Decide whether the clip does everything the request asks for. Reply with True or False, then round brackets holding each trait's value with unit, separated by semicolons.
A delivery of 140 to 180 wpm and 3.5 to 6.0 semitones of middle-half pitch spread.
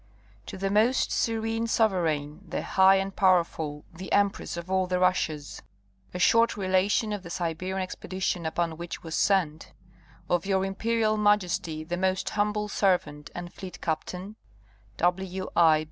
False (145 wpm; 2.9 semitones)